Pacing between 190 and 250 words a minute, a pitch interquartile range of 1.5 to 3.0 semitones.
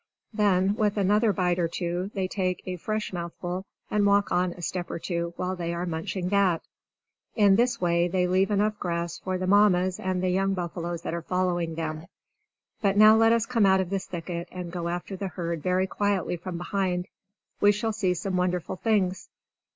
Yes: average, 195 wpm; narrow, 2.4 semitones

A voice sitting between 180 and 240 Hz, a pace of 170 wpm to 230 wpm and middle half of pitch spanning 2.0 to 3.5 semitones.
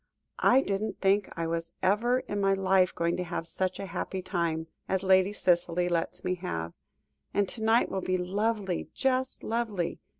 Yes: high, 190 Hz; average, 175 wpm; average, 2.8 semitones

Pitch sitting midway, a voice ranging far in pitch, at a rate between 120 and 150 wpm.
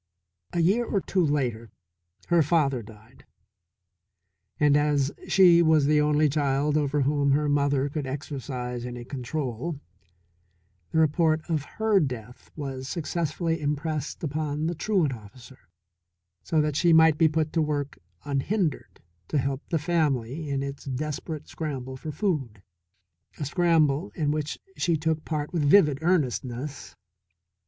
No: medium, 150 Hz; average, 2.8 semitones; average, 140 wpm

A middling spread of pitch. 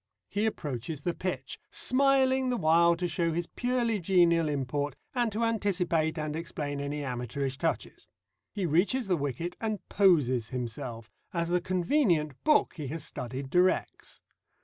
No: wide, 5.8 semitones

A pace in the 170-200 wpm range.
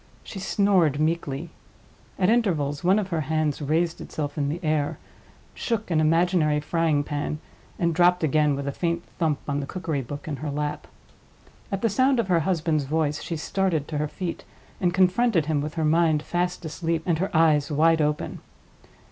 Yes: average, 180 wpm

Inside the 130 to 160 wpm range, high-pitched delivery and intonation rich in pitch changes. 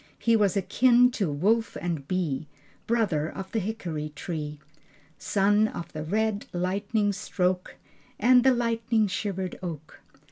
No: slow, 135 wpm; high, 195 Hz; average, 4.6 semitones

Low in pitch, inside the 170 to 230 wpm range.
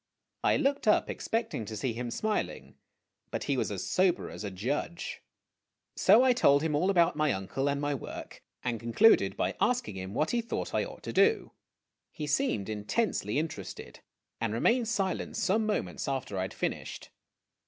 No: medium, 145 Hz; average, 175 wpm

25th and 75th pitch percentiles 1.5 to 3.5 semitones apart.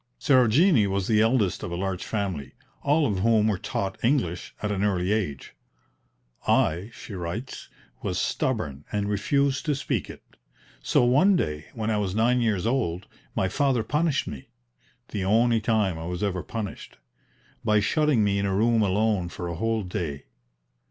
No: average, 4.2 semitones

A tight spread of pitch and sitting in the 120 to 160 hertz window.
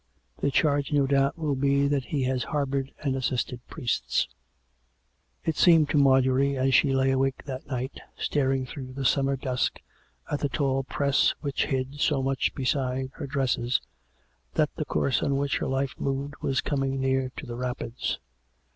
Yes: narrow, 1.3 semitones; low, 135 Hz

